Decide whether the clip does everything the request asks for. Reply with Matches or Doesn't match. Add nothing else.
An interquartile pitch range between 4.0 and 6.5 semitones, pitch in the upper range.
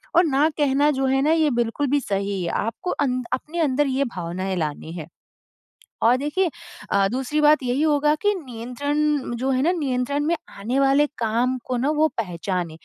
Matches